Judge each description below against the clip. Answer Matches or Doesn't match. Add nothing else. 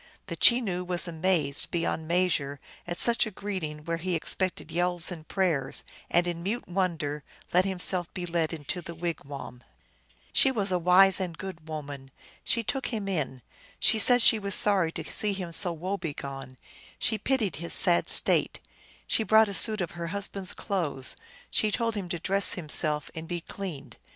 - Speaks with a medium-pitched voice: Matches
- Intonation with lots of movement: Doesn't match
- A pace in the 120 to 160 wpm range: Doesn't match